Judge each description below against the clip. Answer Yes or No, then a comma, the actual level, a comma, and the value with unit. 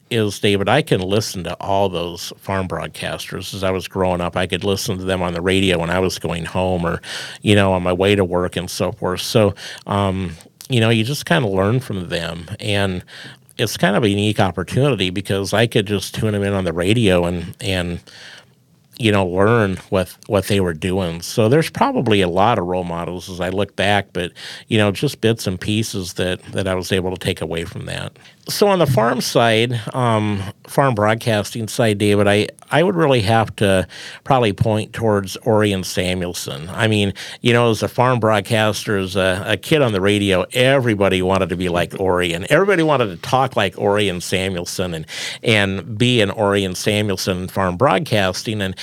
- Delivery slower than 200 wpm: No, fast, 205 wpm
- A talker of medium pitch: No, low, 100 Hz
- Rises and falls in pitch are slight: No, average, 3.2 semitones